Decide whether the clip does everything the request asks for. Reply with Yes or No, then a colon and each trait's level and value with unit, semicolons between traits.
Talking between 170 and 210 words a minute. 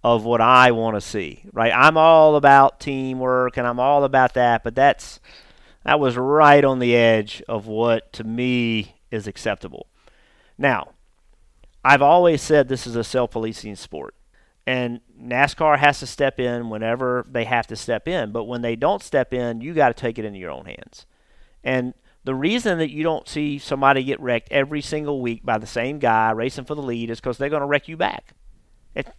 Yes: average, 195 wpm